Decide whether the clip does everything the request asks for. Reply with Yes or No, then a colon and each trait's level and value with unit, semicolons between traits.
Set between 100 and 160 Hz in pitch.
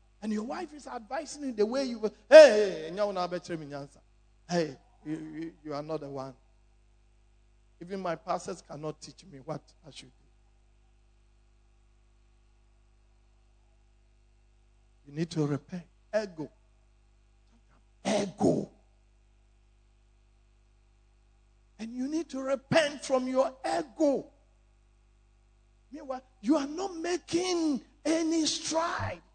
Yes: low, 135 Hz